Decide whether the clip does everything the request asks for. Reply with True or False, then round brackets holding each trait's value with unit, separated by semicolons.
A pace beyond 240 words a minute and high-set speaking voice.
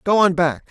False (255 wpm; 175 Hz)